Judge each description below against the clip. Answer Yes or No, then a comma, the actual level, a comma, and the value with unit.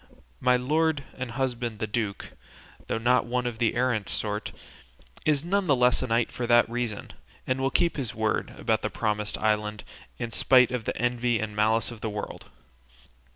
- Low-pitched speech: Yes, low, 120 Hz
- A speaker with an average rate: Yes, average, 185 wpm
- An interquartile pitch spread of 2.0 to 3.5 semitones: Yes, narrow, 2.6 semitones